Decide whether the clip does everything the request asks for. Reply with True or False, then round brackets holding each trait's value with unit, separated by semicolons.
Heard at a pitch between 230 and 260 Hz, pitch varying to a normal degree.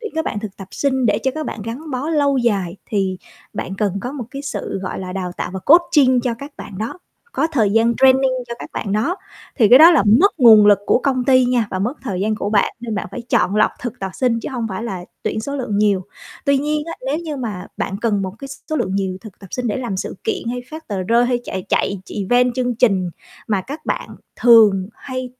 True (235 Hz; 4.9 semitones)